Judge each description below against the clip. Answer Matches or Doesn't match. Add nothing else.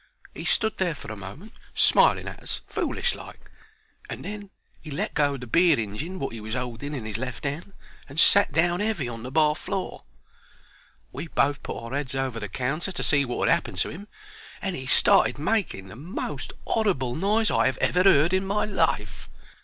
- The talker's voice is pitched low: Doesn't match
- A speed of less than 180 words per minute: Doesn't match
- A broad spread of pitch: Matches